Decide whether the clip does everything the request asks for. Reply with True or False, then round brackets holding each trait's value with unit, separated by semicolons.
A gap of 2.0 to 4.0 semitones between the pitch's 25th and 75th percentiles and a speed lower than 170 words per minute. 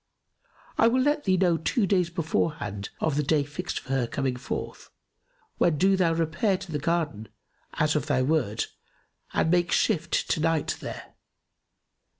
True (3.7 semitones; 160 wpm)